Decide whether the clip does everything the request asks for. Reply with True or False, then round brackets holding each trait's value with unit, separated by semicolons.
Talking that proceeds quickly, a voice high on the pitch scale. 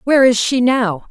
True (215 wpm; 240 Hz)